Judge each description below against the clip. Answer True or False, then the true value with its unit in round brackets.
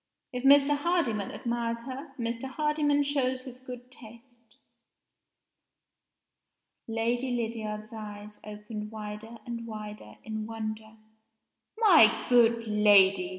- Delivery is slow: True (105 wpm)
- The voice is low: False (230 Hz)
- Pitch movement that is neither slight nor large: True (3.2 semitones)